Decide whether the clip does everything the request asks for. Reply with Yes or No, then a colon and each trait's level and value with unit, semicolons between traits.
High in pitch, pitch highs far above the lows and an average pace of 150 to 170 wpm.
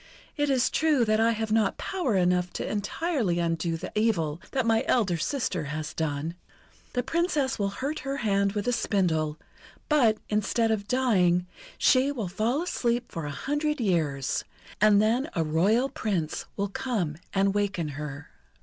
Yes: high, 210 Hz; wide, 6.5 semitones; average, 165 wpm